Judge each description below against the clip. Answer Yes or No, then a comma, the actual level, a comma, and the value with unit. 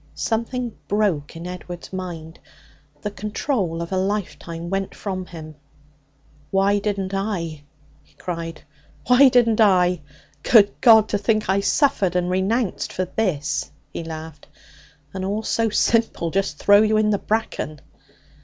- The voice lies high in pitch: Yes, high, 195 Hz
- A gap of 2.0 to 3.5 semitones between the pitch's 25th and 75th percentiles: No, average, 3.9 semitones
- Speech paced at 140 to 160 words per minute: Yes, average, 145 wpm